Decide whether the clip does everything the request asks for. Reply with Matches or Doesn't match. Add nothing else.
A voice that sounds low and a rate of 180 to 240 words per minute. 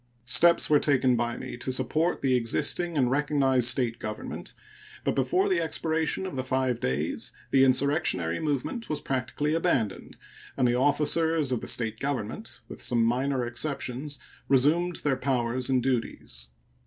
Doesn't match